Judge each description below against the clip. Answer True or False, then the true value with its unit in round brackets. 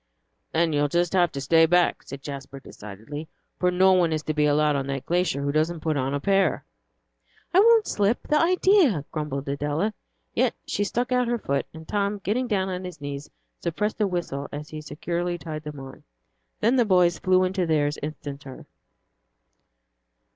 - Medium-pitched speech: True (165 Hz)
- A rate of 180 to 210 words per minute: True (185 wpm)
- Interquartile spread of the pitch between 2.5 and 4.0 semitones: False (4.8 semitones)